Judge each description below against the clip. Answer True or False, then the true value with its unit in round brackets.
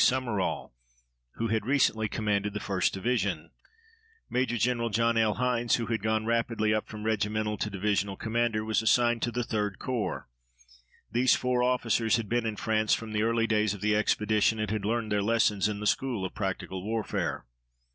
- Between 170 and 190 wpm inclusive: True (180 wpm)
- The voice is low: True (110 Hz)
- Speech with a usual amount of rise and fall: False (1.9 semitones)